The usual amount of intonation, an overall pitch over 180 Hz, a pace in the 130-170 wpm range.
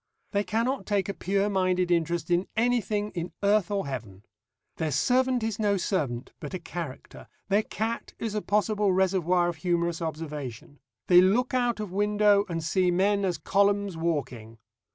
Yes: average, 3.7 semitones; high, 190 Hz; average, 165 wpm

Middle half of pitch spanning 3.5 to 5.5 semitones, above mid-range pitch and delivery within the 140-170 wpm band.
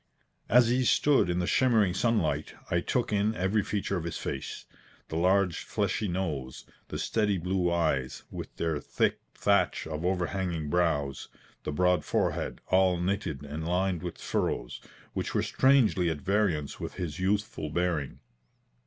No: average, 3.8 semitones; very low, 90 Hz; average, 155 wpm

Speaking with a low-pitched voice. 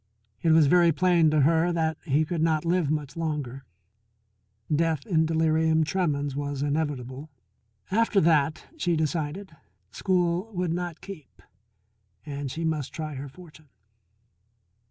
No: medium, 160 Hz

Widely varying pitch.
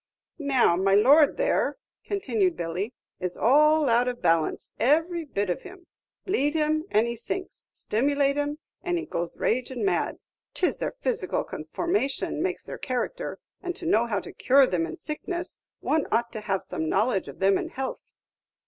Yes: wide, 7.1 semitones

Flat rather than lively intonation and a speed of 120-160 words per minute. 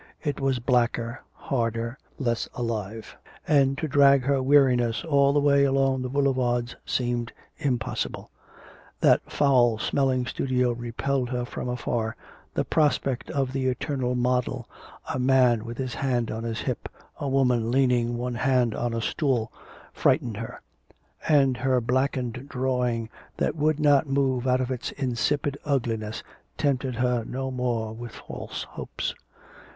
Yes: narrow, 2.3 semitones; average, 145 wpm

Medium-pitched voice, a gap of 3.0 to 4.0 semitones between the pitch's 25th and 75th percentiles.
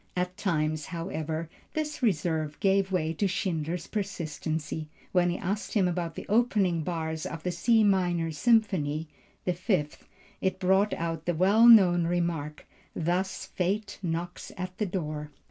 Yes: medium, 175 Hz; average, 3.3 semitones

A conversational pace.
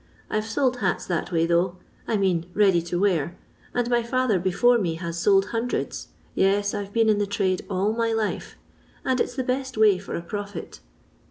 No: fast, 220 wpm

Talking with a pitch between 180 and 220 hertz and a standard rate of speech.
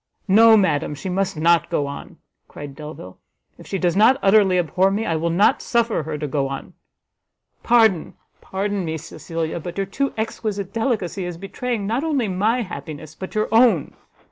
Yes: high, 190 Hz; average, 175 wpm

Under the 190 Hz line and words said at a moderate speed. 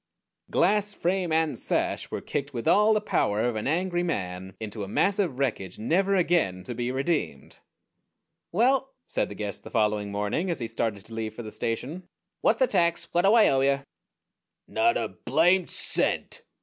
Yes: medium, 140 Hz; average, 185 wpm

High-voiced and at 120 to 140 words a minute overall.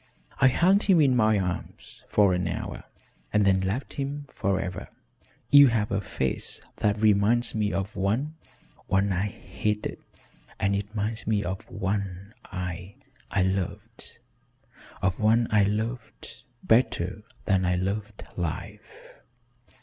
No: low, 105 Hz; slow, 135 wpm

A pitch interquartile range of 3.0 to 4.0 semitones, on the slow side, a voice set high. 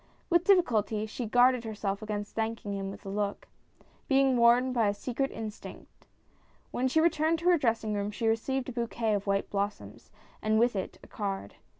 No: average, 3.7 semitones; average, 185 wpm; high, 225 Hz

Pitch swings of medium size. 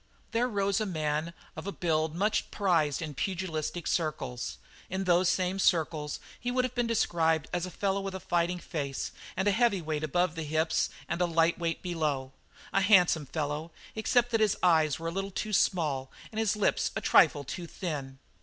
Yes: average, 3.9 semitones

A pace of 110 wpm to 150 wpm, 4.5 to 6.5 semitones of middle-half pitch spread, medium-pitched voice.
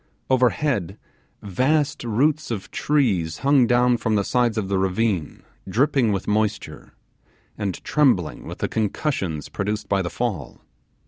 No: slow, 135 wpm; average, 4.9 semitones; low, 110 Hz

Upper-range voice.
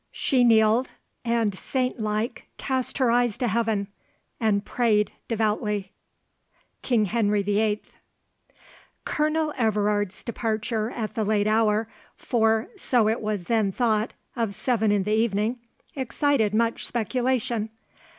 Yes: high, 220 Hz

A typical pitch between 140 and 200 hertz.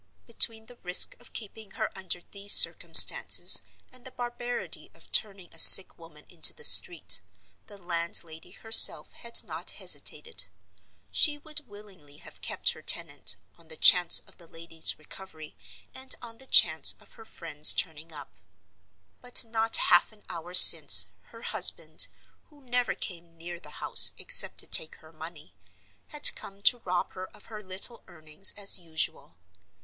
Yes: medium, 185 Hz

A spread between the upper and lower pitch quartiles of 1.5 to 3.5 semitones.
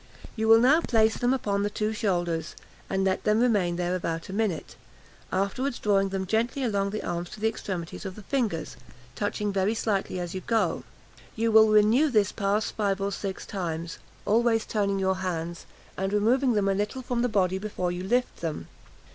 Yes: average, 2.9 semitones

